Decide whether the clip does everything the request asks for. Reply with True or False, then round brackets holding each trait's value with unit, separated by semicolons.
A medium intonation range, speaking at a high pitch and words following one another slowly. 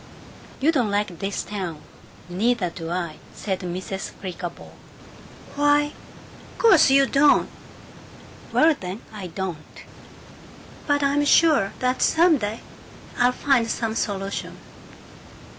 False (7.3 semitones; 215 Hz; 115 wpm)